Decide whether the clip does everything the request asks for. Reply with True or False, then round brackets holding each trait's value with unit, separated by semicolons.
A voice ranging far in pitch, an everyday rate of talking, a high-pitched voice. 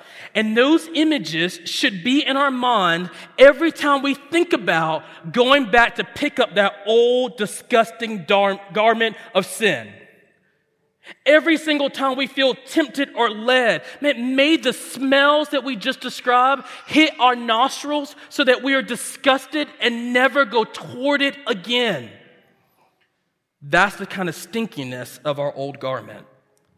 True (5.7 semitones; 145 wpm; 245 Hz)